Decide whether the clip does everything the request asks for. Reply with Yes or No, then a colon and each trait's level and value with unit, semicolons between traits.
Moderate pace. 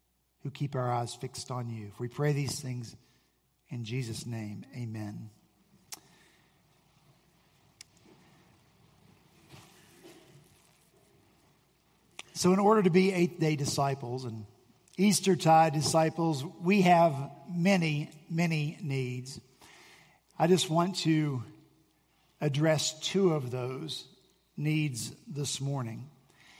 No: slow, 95 wpm